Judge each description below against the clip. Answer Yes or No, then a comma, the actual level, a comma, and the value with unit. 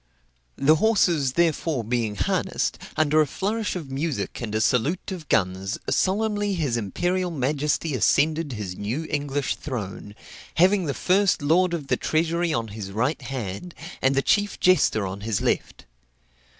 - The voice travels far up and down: Yes, wide, 7.0 semitones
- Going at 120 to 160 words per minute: Yes, average, 150 wpm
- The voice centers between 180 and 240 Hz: No, medium, 145 Hz